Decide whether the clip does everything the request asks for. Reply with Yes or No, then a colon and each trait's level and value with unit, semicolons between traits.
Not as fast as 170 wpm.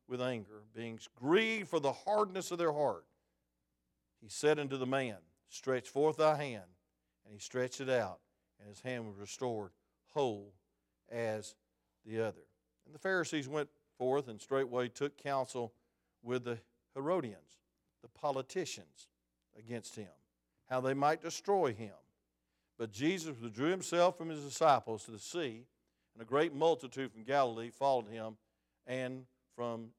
Yes: average, 150 wpm